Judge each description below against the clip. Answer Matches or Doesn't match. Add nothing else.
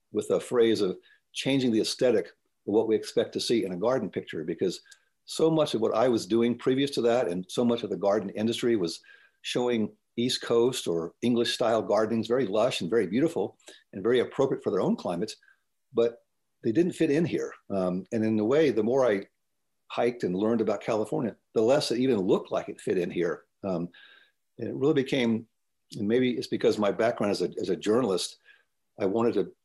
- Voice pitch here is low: Matches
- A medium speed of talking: Doesn't match